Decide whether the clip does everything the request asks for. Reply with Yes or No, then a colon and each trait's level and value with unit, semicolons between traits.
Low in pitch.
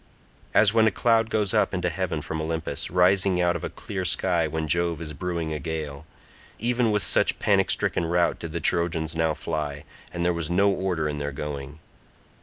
Yes: very low, 85 Hz